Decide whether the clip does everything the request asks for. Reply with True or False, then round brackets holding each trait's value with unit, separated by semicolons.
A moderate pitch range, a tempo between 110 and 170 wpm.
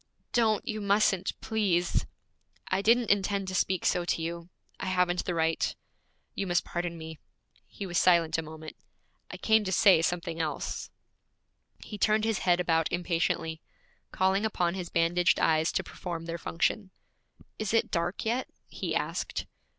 True (3.2 semitones; 160 wpm)